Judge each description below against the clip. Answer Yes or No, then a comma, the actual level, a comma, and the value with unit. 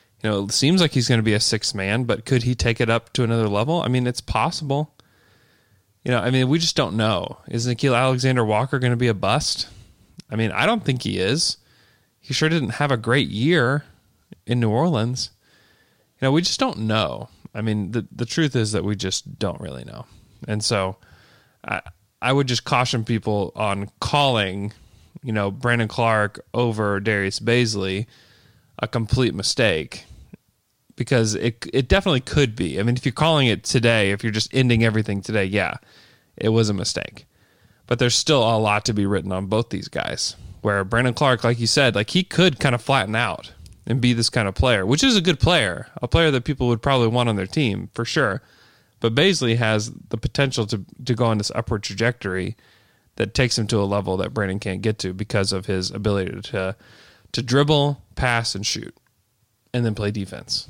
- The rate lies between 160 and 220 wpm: Yes, average, 200 wpm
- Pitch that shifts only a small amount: No, average, 3.7 semitones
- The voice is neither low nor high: No, low, 115 Hz